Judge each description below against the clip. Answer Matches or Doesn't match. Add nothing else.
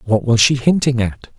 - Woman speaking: Doesn't match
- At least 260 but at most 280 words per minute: Doesn't match